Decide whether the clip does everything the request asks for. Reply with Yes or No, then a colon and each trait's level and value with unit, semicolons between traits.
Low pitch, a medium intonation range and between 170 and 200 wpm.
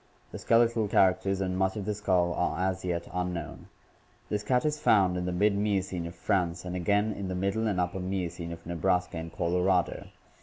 No: very low, 95 Hz; narrow, 2.3 semitones; average, 195 wpm